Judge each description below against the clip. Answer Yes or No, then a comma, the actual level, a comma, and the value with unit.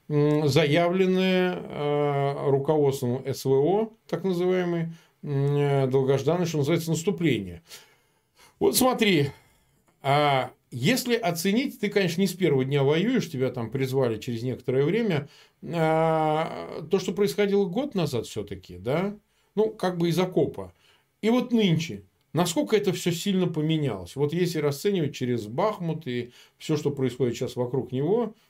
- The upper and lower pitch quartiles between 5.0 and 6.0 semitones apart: Yes, wide, 5.5 semitones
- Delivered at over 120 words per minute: Yes, average, 130 wpm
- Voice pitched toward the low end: No, medium, 155 Hz